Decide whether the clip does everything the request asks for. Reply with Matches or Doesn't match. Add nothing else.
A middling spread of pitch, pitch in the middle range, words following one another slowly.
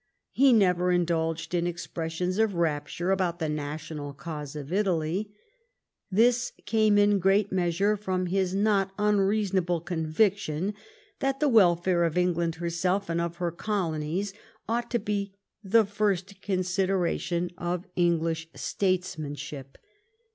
Matches